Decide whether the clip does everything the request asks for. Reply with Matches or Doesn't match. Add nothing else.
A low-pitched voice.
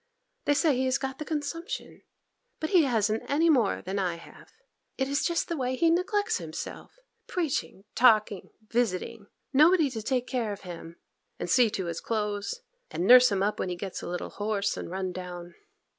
Doesn't match